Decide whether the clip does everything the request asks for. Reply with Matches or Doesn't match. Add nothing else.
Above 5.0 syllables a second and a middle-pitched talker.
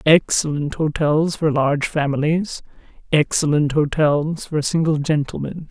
Doesn't match